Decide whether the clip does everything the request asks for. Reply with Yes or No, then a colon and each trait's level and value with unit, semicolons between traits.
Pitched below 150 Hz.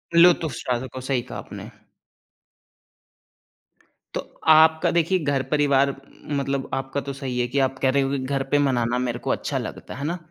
Yes: low, 135 Hz